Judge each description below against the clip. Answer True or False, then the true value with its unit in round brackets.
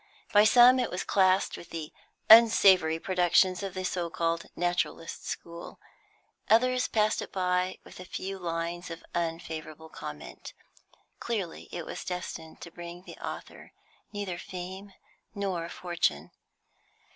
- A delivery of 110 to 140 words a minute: True (135 wpm)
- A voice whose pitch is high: False (180 Hz)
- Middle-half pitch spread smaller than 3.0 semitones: True (2.6 semitones)